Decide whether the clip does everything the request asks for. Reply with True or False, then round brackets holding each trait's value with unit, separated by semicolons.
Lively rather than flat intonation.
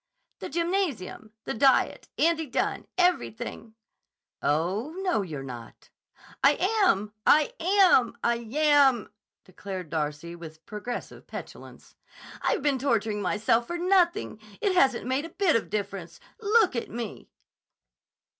True (8.7 semitones)